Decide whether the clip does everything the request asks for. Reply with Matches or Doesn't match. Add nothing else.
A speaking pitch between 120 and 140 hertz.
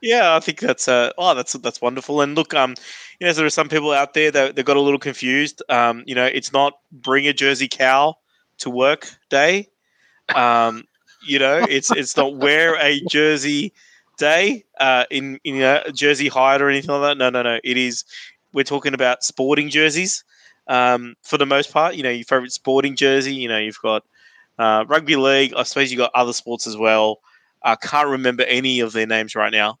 Matches